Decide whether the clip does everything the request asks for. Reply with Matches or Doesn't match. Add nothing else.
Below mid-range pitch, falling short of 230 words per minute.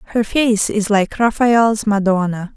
Doesn't match